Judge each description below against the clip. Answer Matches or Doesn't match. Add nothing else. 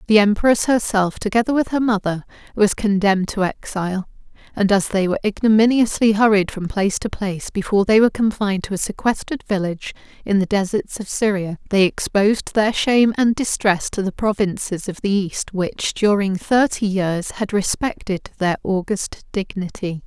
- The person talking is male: Doesn't match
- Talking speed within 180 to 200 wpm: Doesn't match